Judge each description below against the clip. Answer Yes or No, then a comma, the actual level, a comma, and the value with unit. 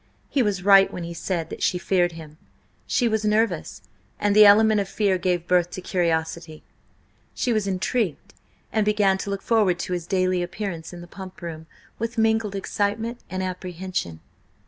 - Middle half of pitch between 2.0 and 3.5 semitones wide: Yes, average, 3.2 semitones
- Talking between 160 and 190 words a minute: Yes, average, 175 wpm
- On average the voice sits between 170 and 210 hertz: Yes, high, 190 Hz